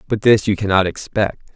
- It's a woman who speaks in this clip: No, male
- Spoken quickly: No, average, 195 wpm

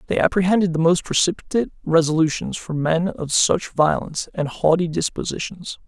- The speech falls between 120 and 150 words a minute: Yes, average, 145 wpm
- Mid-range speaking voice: Yes, medium, 170 Hz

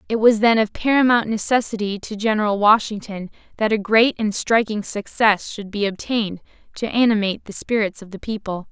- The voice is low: No, high, 215 Hz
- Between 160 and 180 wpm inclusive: Yes, average, 170 wpm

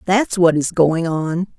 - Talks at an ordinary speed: Yes, average, 190 wpm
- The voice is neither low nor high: Yes, medium, 175 Hz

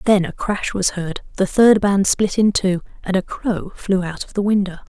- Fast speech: Yes, fast, 230 wpm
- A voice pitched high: Yes, high, 195 Hz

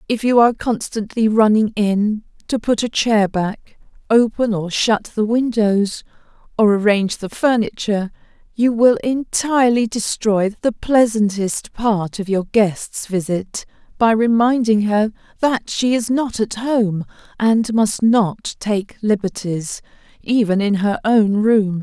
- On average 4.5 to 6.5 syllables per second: No, 3.9 syllables/s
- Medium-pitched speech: No, high, 215 Hz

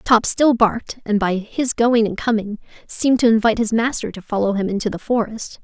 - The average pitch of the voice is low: No, high, 220 Hz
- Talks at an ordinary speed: No, fast, 215 wpm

